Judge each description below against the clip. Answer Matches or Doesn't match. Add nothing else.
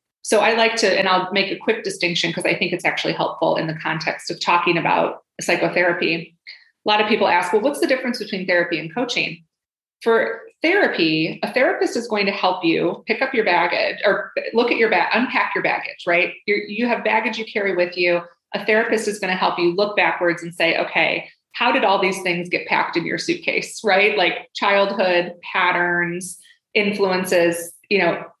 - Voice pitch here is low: Doesn't match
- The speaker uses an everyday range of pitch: Matches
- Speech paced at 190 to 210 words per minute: Matches